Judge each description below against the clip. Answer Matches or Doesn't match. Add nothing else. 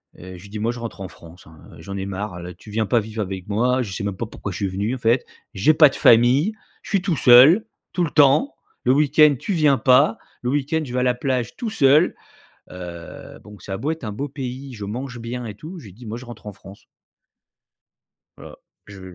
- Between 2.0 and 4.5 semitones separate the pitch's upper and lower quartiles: Doesn't match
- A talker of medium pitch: Doesn't match